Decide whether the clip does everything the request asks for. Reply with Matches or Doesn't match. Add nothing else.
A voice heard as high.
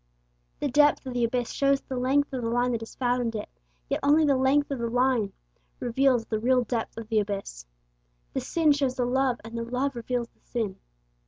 Matches